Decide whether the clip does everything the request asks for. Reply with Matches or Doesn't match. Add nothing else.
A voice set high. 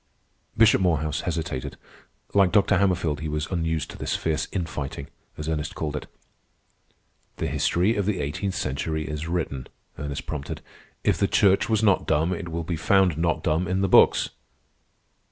Doesn't match